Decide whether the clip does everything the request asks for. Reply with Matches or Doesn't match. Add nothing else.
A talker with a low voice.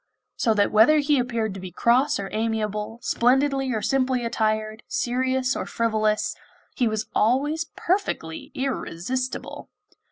Doesn't match